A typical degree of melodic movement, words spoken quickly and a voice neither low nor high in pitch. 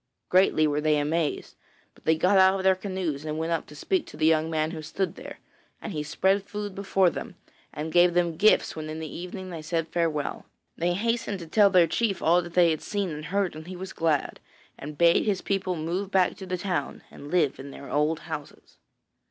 Yes: average, 3.4 semitones; fast, 225 wpm; medium, 170 Hz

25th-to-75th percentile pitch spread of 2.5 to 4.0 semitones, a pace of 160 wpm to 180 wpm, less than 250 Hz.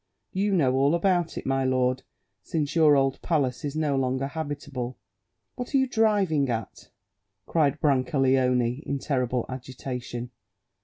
No: average, 3.6 semitones; average, 140 wpm; low, 135 Hz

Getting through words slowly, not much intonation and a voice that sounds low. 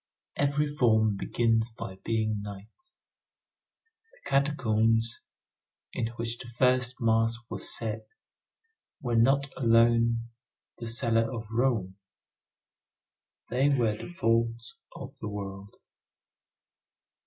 Yes: slow, 100 wpm; narrow, 2.0 semitones; low, 115 Hz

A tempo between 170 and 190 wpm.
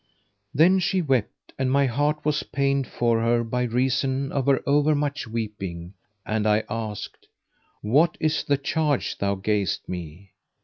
No: average, 150 wpm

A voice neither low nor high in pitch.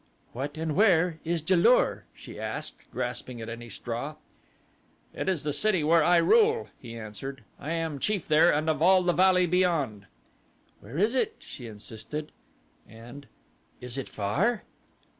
Yes: medium, 155 Hz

